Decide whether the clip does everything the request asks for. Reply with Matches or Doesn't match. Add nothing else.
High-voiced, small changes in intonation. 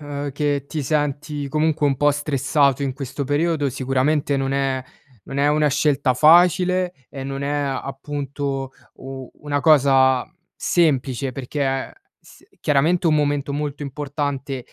Doesn't match